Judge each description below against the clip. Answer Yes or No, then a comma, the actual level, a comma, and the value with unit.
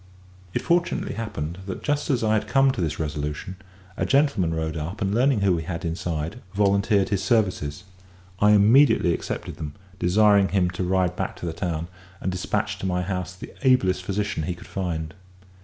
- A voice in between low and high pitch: No, very low, 95 Hz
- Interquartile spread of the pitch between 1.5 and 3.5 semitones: No, average, 3.9 semitones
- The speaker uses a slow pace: No, average, 185 wpm